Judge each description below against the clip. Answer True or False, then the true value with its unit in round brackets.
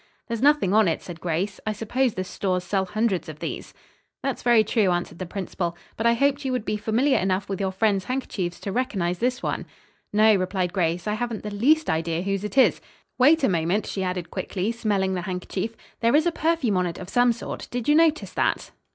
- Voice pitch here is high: True (205 Hz)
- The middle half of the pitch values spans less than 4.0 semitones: False (4.7 semitones)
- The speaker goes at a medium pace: False (220 wpm)